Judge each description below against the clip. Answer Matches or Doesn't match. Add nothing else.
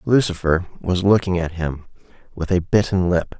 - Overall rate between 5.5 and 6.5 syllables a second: Doesn't match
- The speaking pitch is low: Matches